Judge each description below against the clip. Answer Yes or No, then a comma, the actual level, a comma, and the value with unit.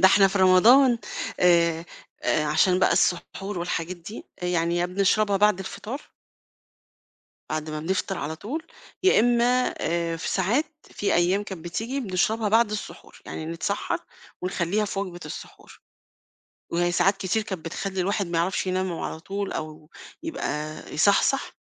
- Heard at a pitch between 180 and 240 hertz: Yes, high, 190 Hz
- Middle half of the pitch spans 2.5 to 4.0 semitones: Yes, average, 3.4 semitones